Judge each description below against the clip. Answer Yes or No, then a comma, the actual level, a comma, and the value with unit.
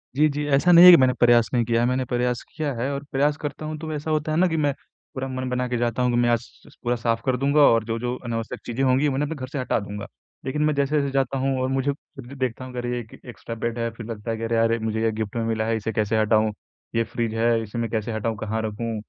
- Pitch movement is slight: No, average, 3.2 semitones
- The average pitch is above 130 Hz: No, low, 120 Hz